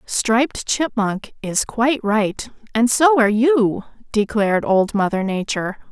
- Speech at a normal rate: No, slow, 130 wpm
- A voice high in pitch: Yes, high, 225 Hz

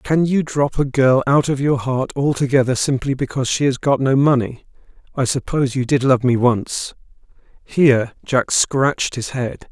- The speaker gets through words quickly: No, average, 180 wpm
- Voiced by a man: Yes, male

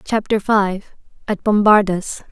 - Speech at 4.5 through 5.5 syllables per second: No, 3.8 syllables/s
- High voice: Yes, high, 205 Hz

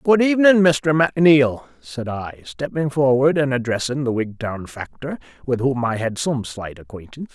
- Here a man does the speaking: Yes, male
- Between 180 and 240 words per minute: No, average, 165 wpm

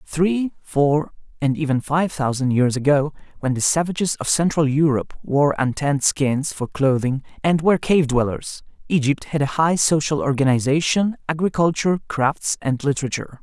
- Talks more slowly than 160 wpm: Yes, average, 150 wpm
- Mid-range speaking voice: Yes, medium, 145 Hz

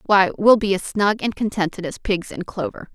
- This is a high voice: Yes, high, 195 Hz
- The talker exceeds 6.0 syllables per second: No, 5.1 syllables/s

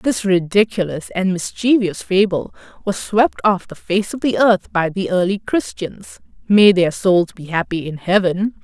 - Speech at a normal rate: Yes, average, 160 wpm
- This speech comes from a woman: Yes, female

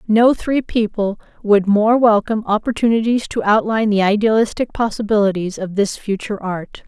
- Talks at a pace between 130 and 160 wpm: Yes, average, 140 wpm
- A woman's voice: Yes, female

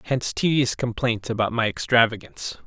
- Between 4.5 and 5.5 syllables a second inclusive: No, 5.7 syllables/s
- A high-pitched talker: No, low, 115 Hz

